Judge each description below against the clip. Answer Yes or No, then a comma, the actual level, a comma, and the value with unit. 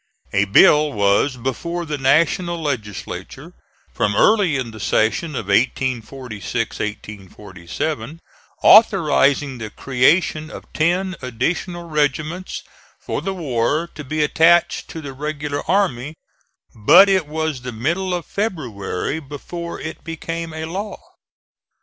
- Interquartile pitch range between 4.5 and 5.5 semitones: Yes, average, 5.1 semitones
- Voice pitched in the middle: Yes, medium, 150 Hz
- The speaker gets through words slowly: Yes, slow, 120 wpm